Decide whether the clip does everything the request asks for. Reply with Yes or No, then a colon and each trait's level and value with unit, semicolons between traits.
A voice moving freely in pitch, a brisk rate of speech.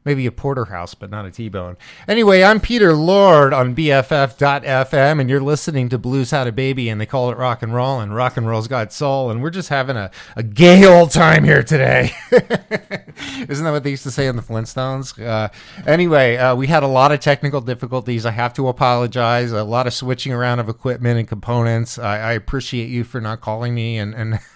No: average, 3.3 semitones; fast, 215 wpm